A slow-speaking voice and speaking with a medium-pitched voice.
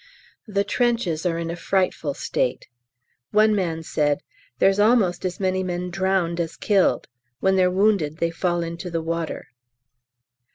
No: average, 150 wpm; medium, 180 Hz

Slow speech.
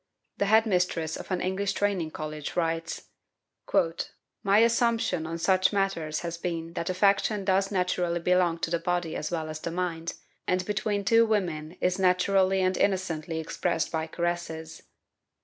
No: average, 160 wpm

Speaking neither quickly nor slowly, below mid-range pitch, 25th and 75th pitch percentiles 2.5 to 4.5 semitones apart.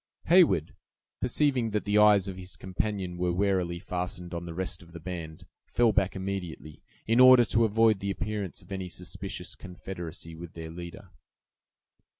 Yes: average, 160 wpm; very low, 95 Hz; average, 3.4 semitones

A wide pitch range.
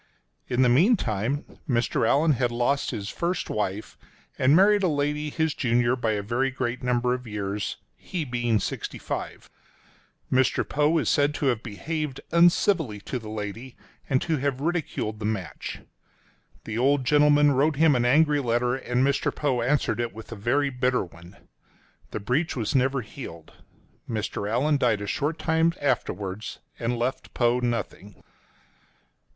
No: average, 4.4 semitones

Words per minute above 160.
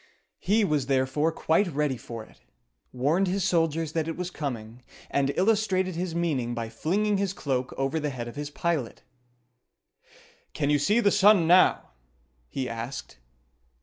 No: average, 155 wpm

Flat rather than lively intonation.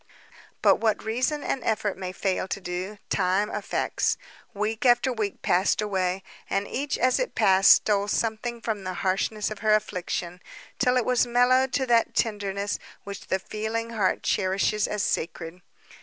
No: average, 3.4 semitones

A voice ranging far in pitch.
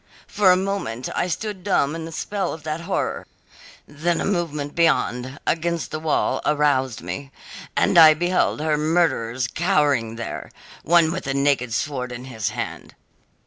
No: average, 4.6 semitones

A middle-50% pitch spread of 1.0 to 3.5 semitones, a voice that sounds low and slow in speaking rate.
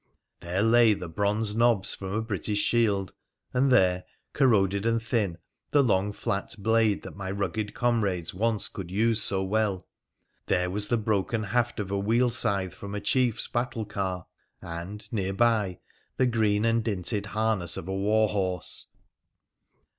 No: average, 2.8 semitones; low, 105 Hz; average, 160 wpm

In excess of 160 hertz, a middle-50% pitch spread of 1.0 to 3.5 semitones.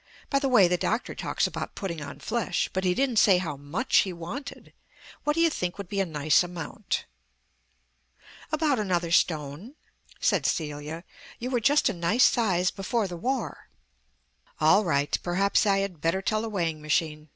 No: medium, 185 Hz; wide, 5.5 semitones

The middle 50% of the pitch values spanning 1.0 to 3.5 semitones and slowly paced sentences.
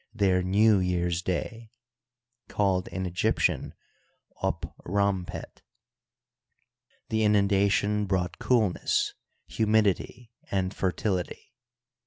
Yes: narrow, 2.4 semitones; slow, 80 wpm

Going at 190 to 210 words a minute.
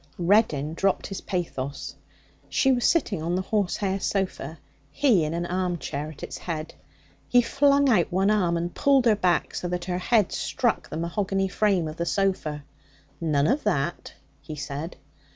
No: average, 170 wpm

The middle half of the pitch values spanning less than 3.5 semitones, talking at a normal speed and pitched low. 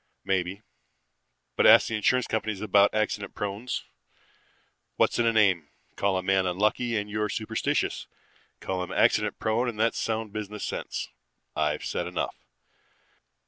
Yes: narrow, 2.4 semitones; average, 145 wpm; low, 105 Hz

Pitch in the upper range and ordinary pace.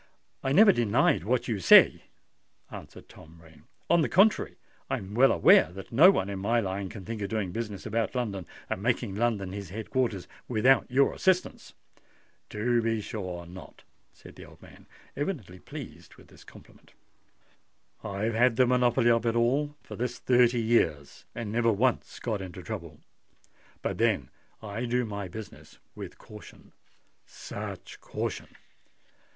No: low, 110 Hz; average, 155 wpm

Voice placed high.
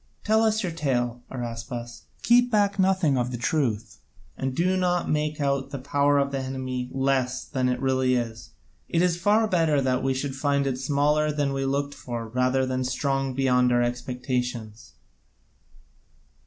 No: low, 135 Hz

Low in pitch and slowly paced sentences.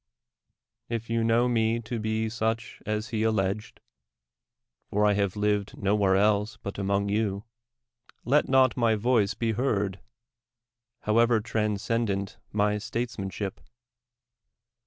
Yes: low, 110 Hz; slow, 130 wpm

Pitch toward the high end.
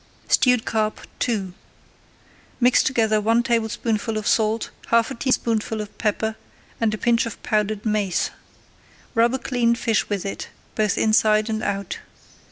Yes: high, 220 Hz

